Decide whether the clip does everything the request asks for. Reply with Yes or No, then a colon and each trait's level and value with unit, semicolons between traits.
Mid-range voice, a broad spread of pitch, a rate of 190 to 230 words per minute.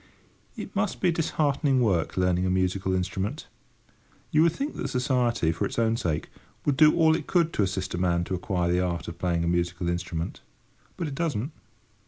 No: very low, 95 Hz; wide, 8.3 semitones; average, 195 wpm